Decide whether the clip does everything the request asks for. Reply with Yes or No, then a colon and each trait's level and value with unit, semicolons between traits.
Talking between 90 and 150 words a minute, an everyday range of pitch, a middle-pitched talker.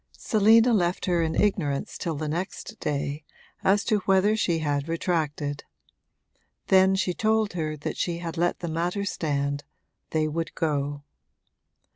Yes: average, 145 wpm; average, 4.2 semitones; medium, 165 Hz